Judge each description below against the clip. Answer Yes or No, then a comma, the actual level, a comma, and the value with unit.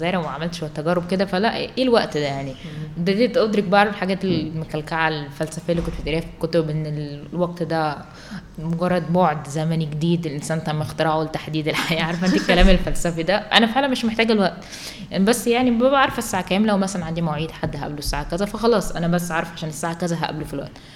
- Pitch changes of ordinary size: Yes, average, 3.4 semitones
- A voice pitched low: No, medium, 165 Hz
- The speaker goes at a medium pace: No, fast, 190 wpm